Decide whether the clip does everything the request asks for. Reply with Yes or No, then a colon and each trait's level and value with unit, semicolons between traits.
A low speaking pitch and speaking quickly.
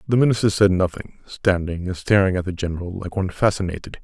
No: very low, 95 Hz; average, 195 wpm